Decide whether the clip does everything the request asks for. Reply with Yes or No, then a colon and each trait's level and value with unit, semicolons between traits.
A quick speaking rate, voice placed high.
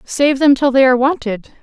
Yes: fast, 220 wpm; very high, 265 Hz